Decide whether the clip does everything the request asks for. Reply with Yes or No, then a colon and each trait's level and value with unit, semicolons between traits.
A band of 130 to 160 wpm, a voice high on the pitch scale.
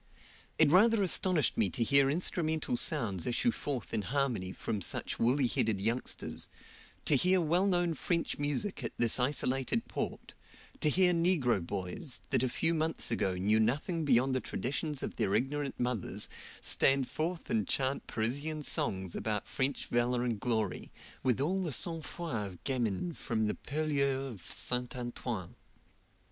No: average, 155 wpm; low, 135 Hz